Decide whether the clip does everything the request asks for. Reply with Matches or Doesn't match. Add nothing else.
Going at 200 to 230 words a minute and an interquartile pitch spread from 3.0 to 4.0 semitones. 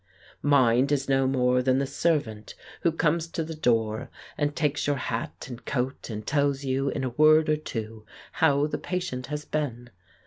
Doesn't match